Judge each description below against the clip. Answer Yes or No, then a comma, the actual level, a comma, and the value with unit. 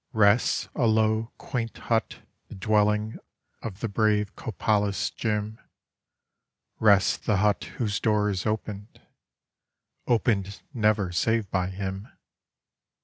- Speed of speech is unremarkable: No, slow, 120 wpm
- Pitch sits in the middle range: No, low, 105 Hz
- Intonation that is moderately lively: No, narrow, 1.6 semitones